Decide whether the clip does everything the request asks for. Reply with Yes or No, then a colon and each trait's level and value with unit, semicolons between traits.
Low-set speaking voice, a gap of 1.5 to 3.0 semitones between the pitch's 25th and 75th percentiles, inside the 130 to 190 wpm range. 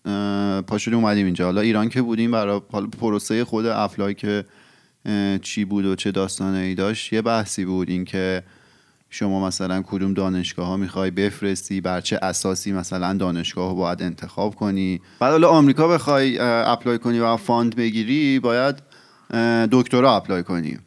No: low, 100 Hz; average, 3.4 semitones; average, 150 wpm